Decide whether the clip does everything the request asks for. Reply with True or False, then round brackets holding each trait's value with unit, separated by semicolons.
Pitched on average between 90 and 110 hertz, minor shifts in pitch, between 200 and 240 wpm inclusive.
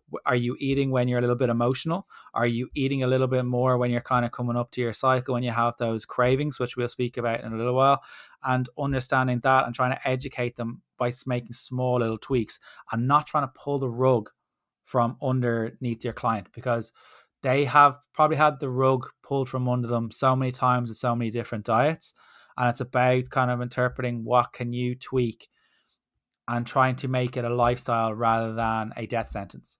False (125 Hz; 1.6 semitones; 205 wpm)